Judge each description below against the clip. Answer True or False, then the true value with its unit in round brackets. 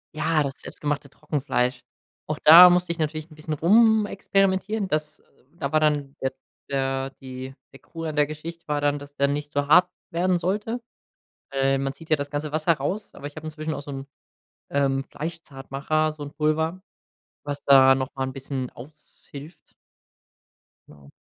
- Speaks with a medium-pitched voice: True (150 Hz)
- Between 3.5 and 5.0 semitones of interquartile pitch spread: False (2.9 semitones)